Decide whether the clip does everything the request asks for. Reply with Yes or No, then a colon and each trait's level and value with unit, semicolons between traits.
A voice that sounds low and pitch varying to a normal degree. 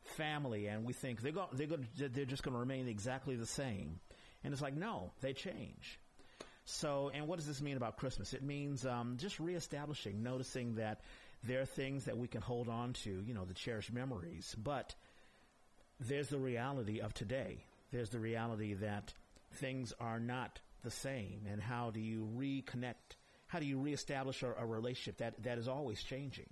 Yes: low, 125 Hz; average, 3.6 semitones